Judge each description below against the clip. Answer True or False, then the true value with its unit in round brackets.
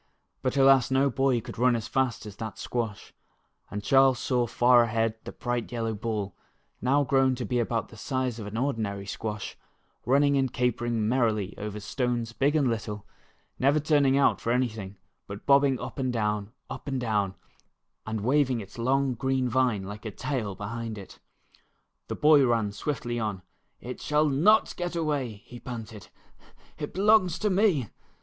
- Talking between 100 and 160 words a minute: False (170 wpm)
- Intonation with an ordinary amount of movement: True (3.7 semitones)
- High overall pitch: False (120 Hz)